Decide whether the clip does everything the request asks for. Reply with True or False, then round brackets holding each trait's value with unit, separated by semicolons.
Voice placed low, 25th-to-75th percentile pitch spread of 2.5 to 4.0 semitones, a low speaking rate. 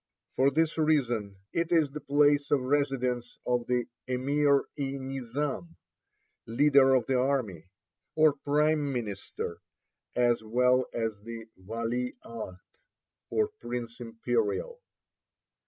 True (130 Hz; 3.6 semitones; 115 wpm)